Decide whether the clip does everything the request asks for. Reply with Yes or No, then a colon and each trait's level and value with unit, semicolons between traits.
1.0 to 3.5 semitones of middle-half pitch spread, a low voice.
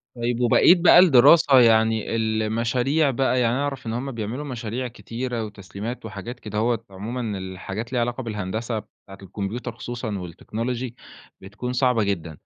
Yes: average, 2.8 semitones; low, 115 Hz